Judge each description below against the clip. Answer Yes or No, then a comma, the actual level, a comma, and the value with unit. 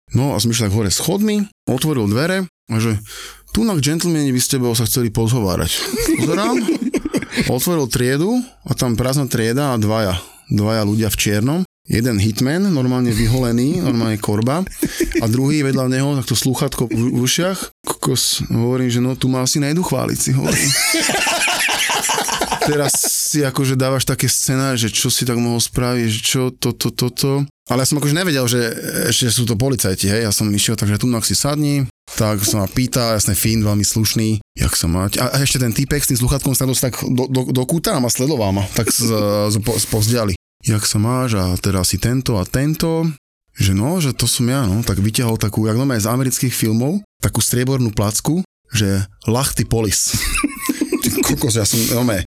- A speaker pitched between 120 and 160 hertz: Yes, low, 125 Hz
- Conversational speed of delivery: No, fast, 185 wpm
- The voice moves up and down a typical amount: Yes, average, 3.9 semitones